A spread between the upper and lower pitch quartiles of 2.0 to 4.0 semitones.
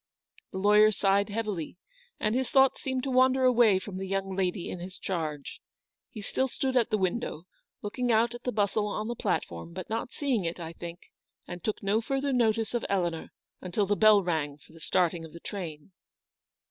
No: average, 4.8 semitones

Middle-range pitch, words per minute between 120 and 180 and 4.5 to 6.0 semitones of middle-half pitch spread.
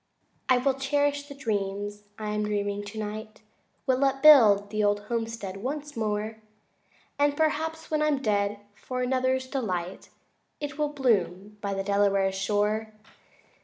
No: high, 220 Hz; average, 140 wpm; average, 4.9 semitones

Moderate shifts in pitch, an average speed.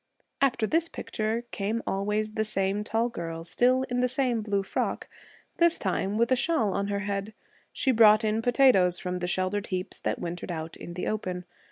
Yes: average, 4.0 semitones; average, 190 wpm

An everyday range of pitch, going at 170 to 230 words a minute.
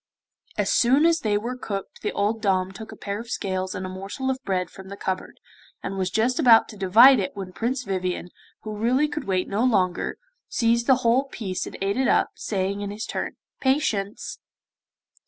Yes: average, 4.5 semitones; average, 200 wpm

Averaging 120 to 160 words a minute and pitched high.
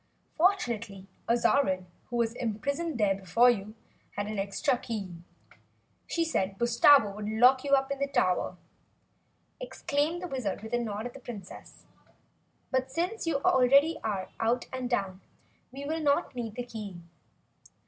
Yes: average, 150 wpm; high, 240 Hz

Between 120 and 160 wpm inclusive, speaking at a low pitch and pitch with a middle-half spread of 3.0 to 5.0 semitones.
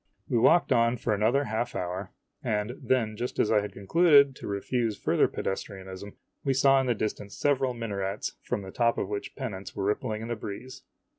No: average, 200 wpm; low, 110 Hz; average, 4.1 semitones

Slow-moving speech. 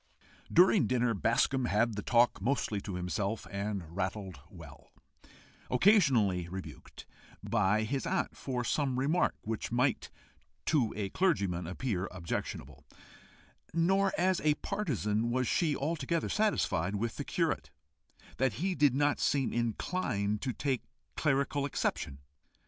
Yes: slow, 125 wpm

